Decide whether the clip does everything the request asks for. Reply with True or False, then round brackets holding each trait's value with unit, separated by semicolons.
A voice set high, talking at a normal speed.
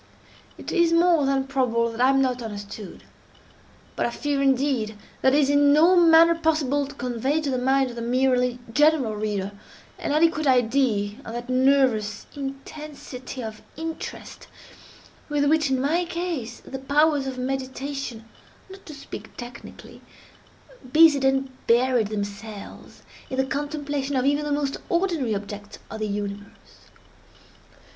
True (270 Hz; 150 wpm)